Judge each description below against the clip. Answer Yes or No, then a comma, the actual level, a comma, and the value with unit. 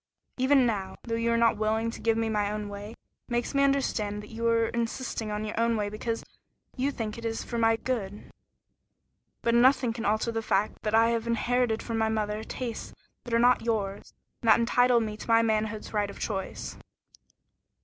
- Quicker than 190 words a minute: Yes, average, 200 wpm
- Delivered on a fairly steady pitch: Yes, narrow, 1.7 semitones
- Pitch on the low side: No, high, 225 Hz